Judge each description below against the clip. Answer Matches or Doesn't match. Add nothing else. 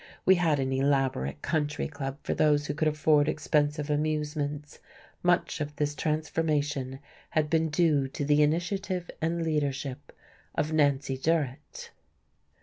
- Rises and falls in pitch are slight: Matches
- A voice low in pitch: Doesn't match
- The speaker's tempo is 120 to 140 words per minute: Matches